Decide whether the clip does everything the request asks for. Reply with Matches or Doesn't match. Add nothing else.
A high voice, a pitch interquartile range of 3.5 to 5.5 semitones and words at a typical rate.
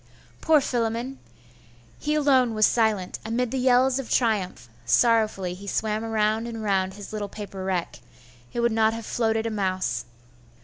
Doesn't match